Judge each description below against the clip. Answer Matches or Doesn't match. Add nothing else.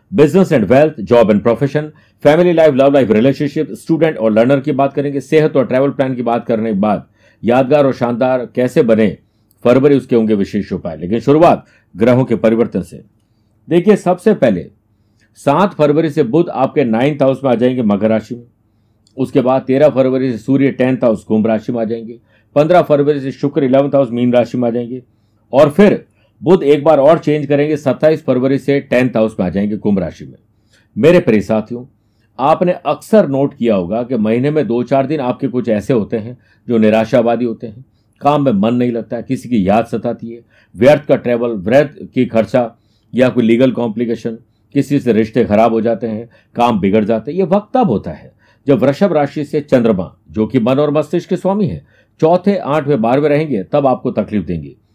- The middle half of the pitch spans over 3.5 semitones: Matches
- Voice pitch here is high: Doesn't match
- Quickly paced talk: Matches